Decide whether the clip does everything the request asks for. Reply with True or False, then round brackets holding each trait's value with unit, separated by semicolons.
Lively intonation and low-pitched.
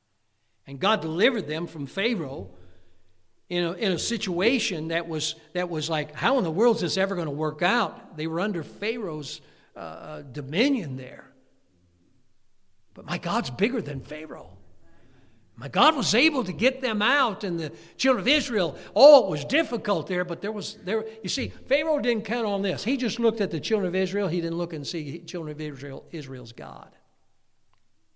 False (8.1 semitones; 170 Hz)